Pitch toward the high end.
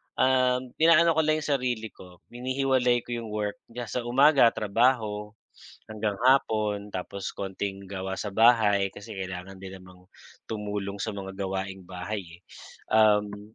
No: low, 105 Hz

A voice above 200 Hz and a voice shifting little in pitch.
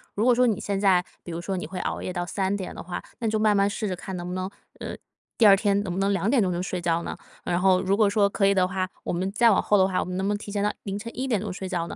No: high, 195 Hz; narrow, 2.1 semitones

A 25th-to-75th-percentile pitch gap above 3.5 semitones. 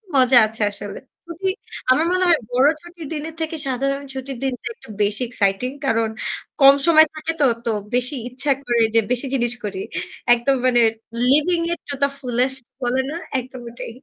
Yes: average, 3.9 semitones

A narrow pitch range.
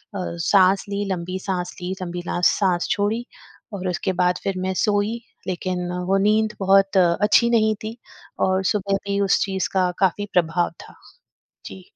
Yes: narrow, 2.1 semitones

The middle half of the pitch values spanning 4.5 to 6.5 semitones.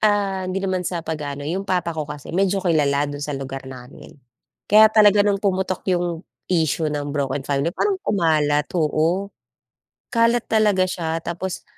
Yes: average, 4.8 semitones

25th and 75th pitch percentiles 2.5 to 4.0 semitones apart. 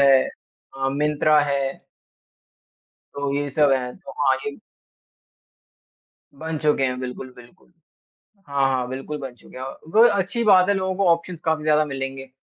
Yes: average, 3.7 semitones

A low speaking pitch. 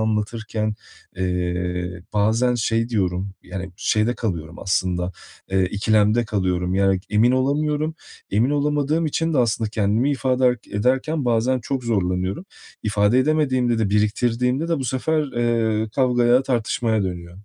Yes: low, 110 Hz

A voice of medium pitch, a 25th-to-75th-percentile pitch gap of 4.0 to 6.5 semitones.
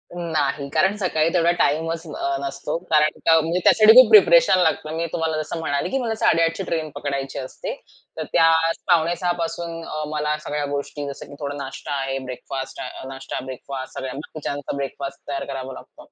No: medium, 155 Hz; average, 3.2 semitones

